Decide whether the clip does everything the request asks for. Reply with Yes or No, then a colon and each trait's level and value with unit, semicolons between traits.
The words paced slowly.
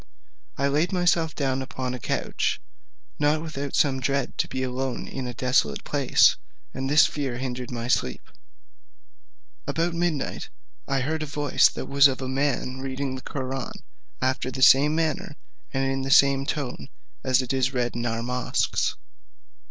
No: average, 165 wpm